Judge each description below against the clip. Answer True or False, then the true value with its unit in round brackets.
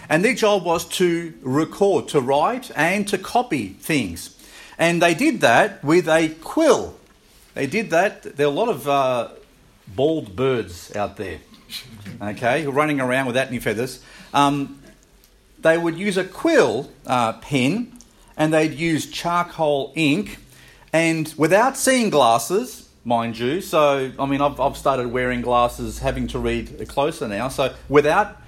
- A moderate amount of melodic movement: False (6.0 semitones)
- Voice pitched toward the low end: False (155 Hz)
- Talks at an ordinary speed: True (155 wpm)